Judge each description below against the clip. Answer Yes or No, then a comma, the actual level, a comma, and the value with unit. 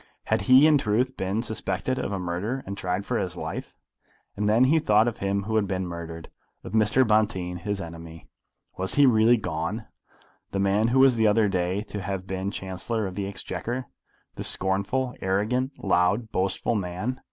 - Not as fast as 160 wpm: No, average, 185 wpm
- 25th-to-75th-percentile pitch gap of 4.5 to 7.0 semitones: No, average, 3.7 semitones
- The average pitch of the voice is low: Yes, low, 100 Hz